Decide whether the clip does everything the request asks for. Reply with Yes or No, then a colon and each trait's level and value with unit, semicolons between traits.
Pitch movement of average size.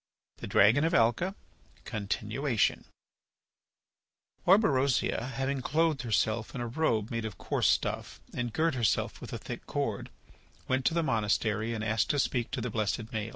Yes: average, 4.2 semitones